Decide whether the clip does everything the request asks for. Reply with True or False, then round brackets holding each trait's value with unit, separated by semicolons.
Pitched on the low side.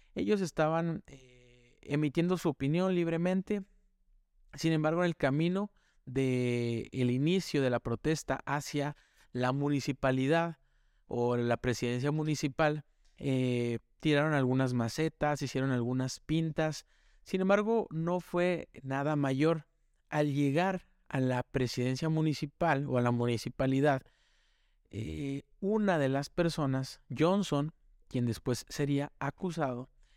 False (145 Hz)